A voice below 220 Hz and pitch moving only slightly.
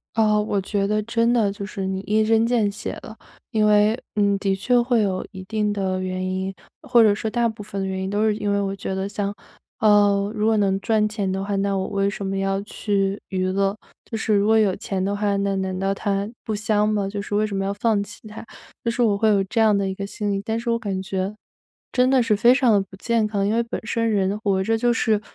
Yes: high, 205 Hz; narrow, 1.9 semitones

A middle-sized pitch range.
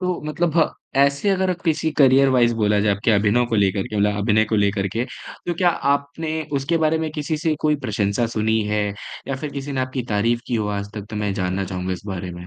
No: wide, 6.0 semitones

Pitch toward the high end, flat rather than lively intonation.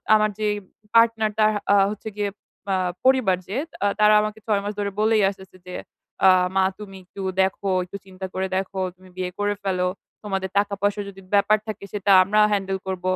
Yes: high, 200 Hz; narrow, 1.9 semitones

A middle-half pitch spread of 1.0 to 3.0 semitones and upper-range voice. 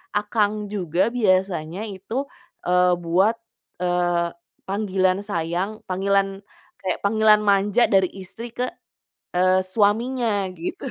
Yes: narrow, 2.4 semitones; high, 195 Hz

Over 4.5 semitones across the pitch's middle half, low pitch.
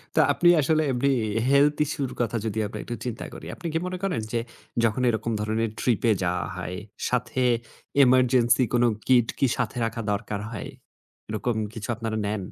No: average, 2.8 semitones; low, 120 Hz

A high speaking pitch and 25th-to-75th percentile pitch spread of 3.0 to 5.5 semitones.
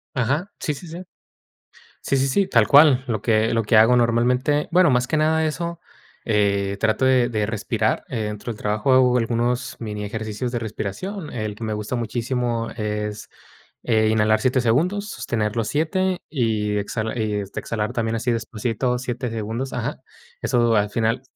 No: low, 115 Hz; average, 3.3 semitones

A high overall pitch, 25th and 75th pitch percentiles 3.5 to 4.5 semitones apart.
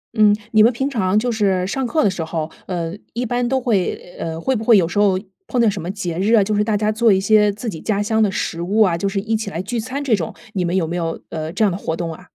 Yes: high, 205 Hz; average, 3.8 semitones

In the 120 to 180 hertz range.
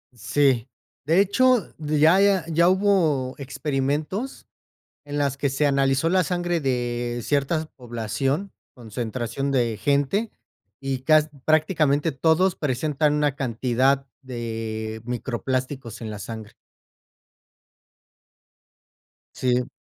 Yes: medium, 140 Hz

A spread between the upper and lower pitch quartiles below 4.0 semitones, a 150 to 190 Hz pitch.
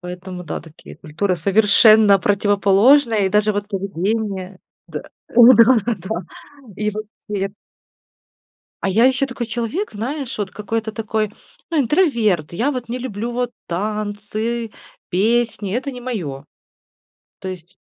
No: average, 3.5 semitones; high, 215 Hz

